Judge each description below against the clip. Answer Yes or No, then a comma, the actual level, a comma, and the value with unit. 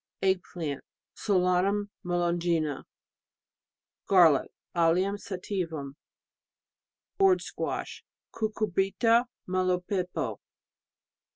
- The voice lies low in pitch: No, medium, 180 Hz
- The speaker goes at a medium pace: No, slow, 60 wpm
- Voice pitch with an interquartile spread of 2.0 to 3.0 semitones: Yes, average, 2.7 semitones